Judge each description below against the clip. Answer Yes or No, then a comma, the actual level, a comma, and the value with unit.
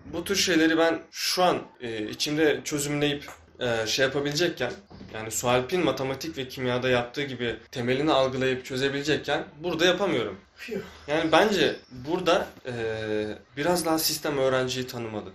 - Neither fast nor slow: Yes, average, 130 wpm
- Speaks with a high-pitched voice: No, low, 135 Hz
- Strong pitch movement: No, average, 4.5 semitones